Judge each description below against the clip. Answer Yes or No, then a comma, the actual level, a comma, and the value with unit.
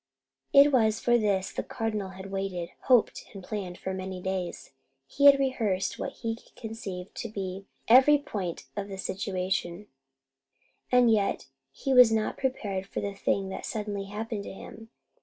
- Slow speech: No, average, 160 wpm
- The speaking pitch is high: Yes, high, 200 Hz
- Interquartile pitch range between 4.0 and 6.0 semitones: No, average, 3.1 semitones